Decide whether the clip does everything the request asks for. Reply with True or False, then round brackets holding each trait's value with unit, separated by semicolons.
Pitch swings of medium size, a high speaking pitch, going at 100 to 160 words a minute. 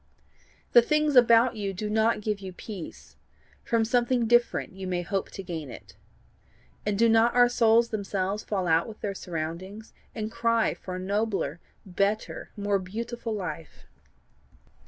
True (3.6 semitones; 210 Hz; 155 wpm)